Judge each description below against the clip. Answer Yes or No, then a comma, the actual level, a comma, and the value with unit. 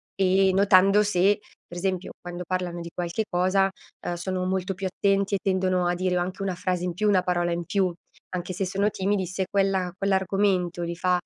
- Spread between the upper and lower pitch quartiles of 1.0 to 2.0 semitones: Yes, narrow, 1.6 semitones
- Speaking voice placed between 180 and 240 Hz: Yes, medium, 185 Hz